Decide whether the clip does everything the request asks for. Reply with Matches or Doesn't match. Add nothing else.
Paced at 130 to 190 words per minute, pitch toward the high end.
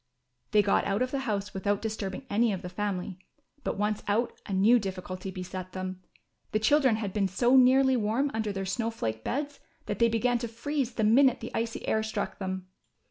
Doesn't match